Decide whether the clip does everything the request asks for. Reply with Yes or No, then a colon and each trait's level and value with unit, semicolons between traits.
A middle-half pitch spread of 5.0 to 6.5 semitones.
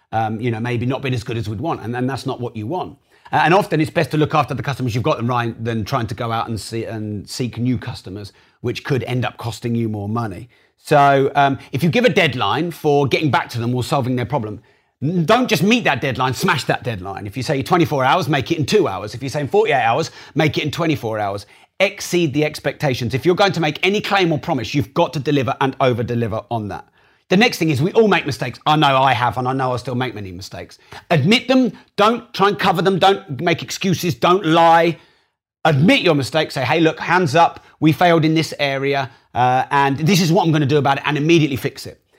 Yes: wide, 5.4 semitones